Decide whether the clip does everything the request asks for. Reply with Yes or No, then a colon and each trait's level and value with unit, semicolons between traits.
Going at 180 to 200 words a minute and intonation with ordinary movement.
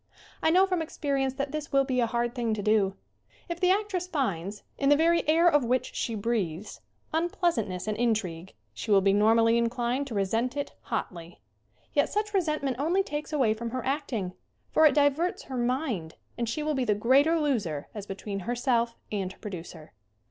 No: average, 190 wpm; wide, 6.2 semitones